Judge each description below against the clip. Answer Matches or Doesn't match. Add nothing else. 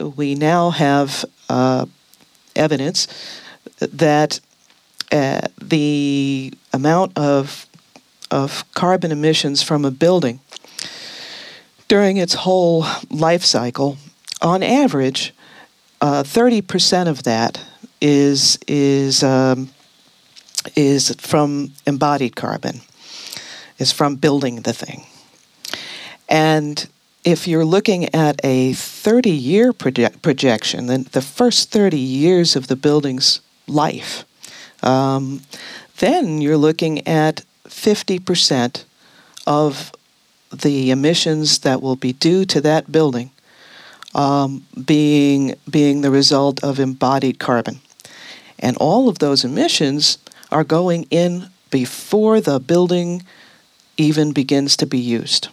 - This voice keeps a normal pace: Doesn't match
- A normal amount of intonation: Matches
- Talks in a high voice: Doesn't match